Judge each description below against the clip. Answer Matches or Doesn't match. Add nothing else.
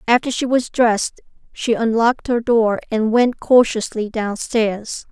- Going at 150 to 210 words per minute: Doesn't match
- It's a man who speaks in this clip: Doesn't match